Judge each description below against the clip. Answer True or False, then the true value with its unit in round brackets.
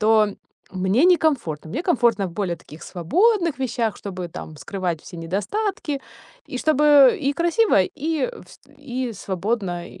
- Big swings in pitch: True (8.2 semitones)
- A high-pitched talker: True (235 Hz)